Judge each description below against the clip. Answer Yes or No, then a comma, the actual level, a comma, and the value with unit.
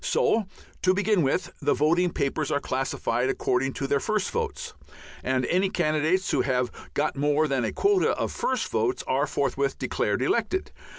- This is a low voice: No, medium, 155 Hz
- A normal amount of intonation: No, wide, 7.3 semitones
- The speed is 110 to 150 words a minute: No, average, 170 wpm